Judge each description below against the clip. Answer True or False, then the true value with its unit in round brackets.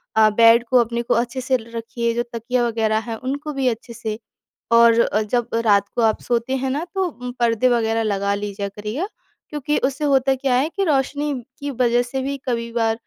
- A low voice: False (240 Hz)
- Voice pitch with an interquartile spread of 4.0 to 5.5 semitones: False (2.7 semitones)